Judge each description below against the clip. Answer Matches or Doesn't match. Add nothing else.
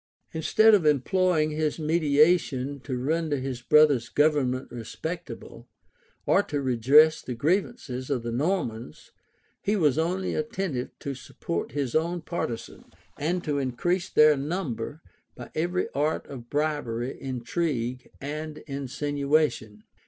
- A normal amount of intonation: Matches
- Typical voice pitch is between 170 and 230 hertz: Doesn't match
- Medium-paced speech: Doesn't match